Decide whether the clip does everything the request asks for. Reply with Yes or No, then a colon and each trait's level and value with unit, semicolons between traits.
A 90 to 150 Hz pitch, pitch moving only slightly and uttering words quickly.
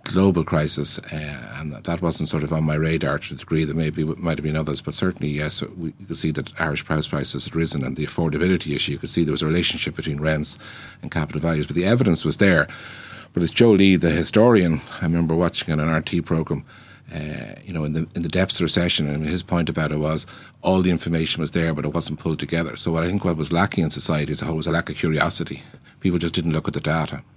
No: very low, 80 Hz; narrow, 1.8 semitones; fast, 255 wpm